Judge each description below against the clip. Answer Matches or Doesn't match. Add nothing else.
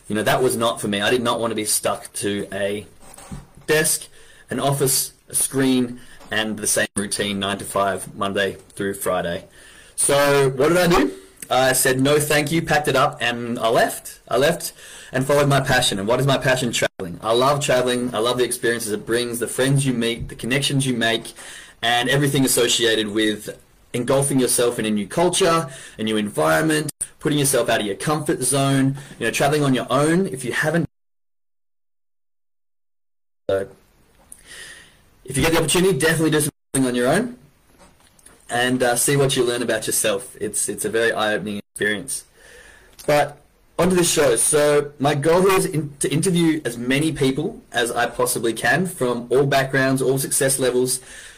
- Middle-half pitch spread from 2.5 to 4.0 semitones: Doesn't match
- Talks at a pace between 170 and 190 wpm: Matches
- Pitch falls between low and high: Doesn't match